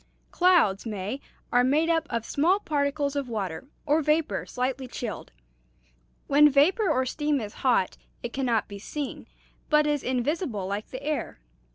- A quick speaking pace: No, average, 160 wpm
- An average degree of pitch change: Yes, average, 4.3 semitones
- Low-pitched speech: No, very high, 275 Hz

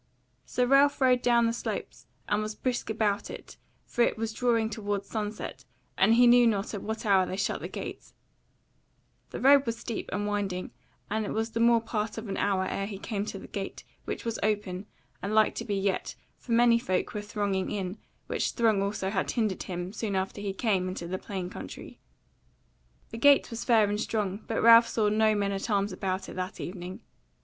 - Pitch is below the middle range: No, high, 210 Hz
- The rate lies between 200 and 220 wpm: Yes, fast, 205 wpm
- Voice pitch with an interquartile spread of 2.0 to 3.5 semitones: Yes, average, 2.7 semitones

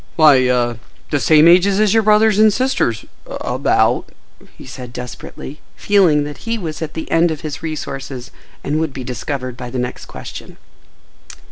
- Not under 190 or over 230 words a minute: No, average, 150 wpm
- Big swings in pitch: Yes, wide, 6.5 semitones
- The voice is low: No, medium, 150 Hz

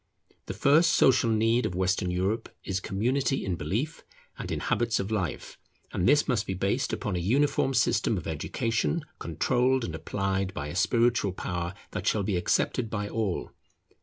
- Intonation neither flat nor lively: Yes, average, 4.8 semitones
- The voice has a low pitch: Yes, low, 105 Hz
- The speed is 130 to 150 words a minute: No, average, 170 wpm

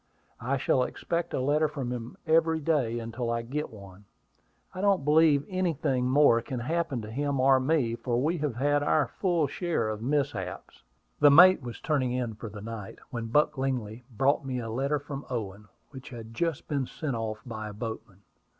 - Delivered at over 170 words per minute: Yes, average, 190 wpm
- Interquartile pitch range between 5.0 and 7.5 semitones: No, average, 4.4 semitones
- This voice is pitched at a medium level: No, low, 130 Hz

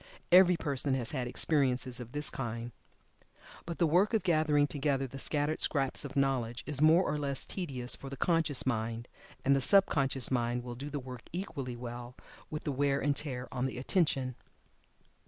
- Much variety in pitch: No, average, 3.2 semitones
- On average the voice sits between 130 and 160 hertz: Yes, low, 135 Hz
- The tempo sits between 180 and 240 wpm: Yes, average, 185 wpm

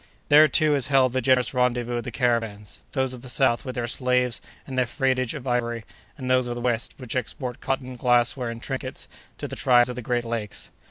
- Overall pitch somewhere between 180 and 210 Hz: No, low, 125 Hz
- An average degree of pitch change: No, narrow, 1.5 semitones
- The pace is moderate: No, fast, 215 wpm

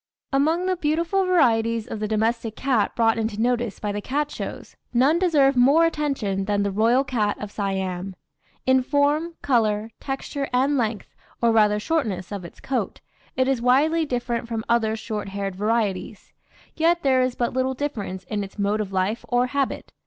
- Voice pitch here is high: Yes, high, 235 Hz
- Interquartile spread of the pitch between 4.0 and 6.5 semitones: Yes, average, 4.8 semitones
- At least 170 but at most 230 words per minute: Yes, average, 175 wpm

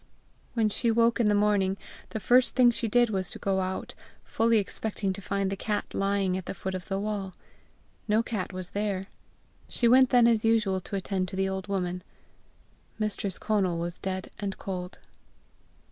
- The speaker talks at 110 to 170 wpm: No, average, 185 wpm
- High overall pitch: Yes, high, 200 Hz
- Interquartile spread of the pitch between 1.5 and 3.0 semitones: Yes, average, 2.7 semitones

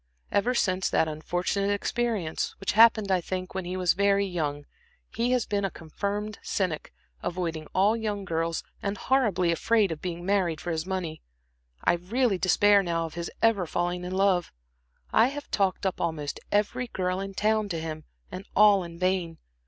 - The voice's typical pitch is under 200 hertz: Yes, medium, 185 Hz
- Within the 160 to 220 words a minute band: Yes, average, 175 wpm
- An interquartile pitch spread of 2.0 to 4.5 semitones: Yes, average, 3.2 semitones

